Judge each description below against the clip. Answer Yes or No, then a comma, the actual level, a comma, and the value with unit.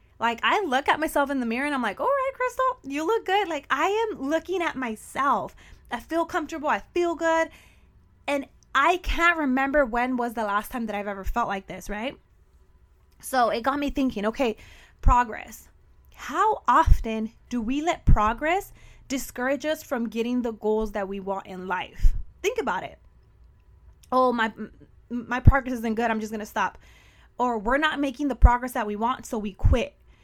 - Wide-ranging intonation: Yes, wide, 5.8 semitones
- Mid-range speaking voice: No, very high, 255 Hz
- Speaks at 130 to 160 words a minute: No, average, 190 wpm